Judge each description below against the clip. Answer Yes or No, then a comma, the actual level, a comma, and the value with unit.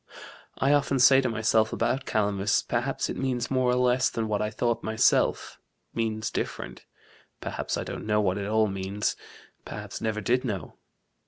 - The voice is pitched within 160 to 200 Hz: No, low, 110 Hz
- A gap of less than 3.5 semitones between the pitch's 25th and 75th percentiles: Yes, average, 3.0 semitones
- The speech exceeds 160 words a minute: Yes, average, 170 wpm